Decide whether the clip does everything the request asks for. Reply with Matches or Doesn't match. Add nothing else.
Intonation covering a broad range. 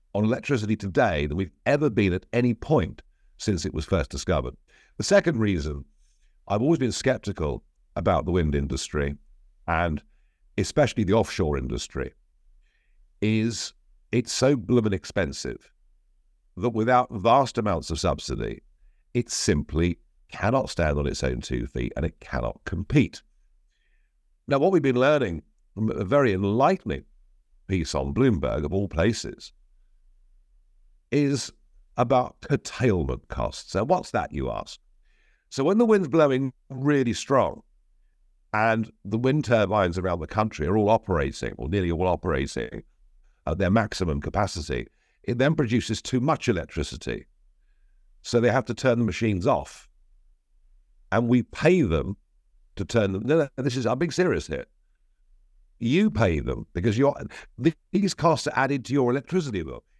Matches